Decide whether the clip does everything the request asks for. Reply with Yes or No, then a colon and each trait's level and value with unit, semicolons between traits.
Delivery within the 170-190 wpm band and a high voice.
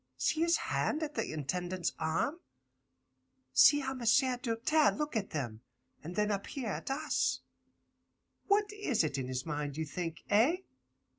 No: average, 155 wpm; high, 215 Hz